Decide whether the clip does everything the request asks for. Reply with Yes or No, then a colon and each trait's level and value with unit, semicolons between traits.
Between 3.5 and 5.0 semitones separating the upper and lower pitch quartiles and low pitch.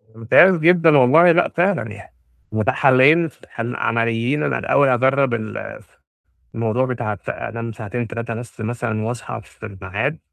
Yes: average, 4.0 semitones; low, 120 Hz